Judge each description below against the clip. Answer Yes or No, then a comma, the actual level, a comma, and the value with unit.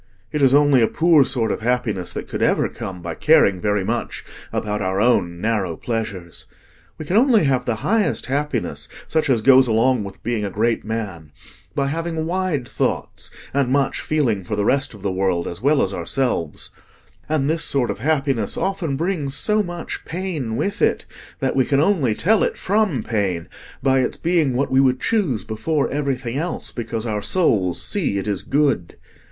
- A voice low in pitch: Yes, low, 130 Hz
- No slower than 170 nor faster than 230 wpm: Yes, average, 185 wpm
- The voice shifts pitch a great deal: Yes, wide, 6.5 semitones